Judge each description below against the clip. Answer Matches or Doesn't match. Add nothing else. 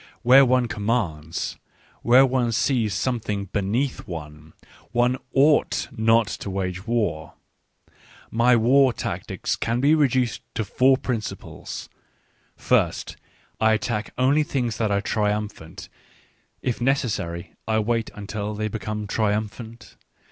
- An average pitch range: Matches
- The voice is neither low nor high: Doesn't match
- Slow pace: Matches